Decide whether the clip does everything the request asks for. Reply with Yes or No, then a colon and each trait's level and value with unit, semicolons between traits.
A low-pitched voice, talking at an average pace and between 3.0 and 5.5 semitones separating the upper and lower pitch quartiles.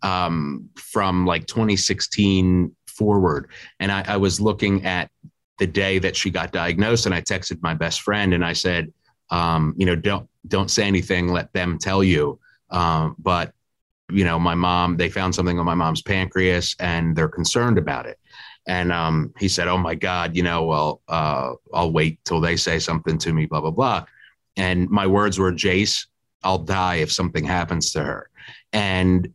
No: very low, 90 Hz; average, 185 wpm; narrow, 2.4 semitones